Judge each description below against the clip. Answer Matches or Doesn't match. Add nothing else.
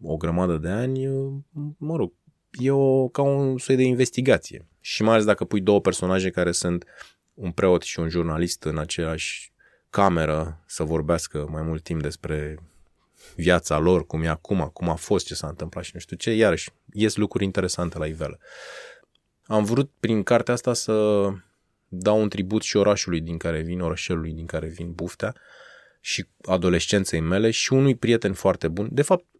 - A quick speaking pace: Matches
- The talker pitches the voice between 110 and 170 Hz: Doesn't match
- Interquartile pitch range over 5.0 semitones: Matches